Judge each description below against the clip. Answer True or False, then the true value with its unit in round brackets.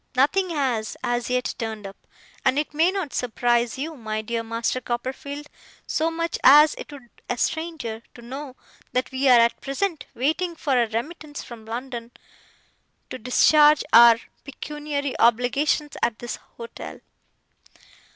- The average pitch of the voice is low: False (255 Hz)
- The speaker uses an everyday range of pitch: True (4.1 semitones)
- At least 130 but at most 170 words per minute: True (145 wpm)